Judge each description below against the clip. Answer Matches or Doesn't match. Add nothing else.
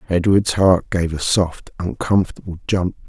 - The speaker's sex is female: Doesn't match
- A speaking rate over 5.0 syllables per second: Doesn't match